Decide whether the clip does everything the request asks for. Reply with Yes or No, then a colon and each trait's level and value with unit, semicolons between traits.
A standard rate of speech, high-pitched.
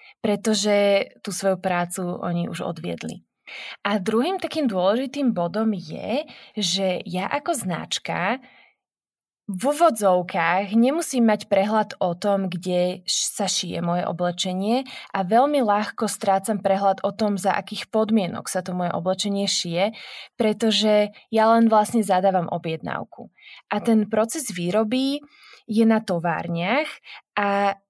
Yes: average, 125 wpm; high, 205 Hz